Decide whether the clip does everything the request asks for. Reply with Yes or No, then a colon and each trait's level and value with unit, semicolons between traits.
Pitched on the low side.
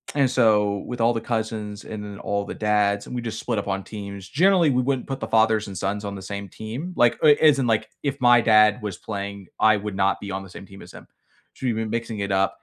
Yes: low, 110 Hz